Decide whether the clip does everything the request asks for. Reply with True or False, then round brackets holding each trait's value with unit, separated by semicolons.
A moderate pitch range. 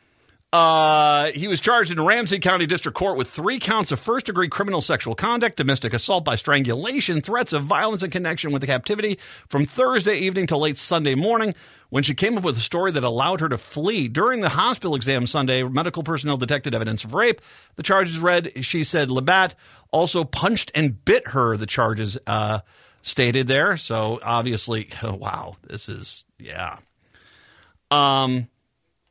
False (6.5 semitones)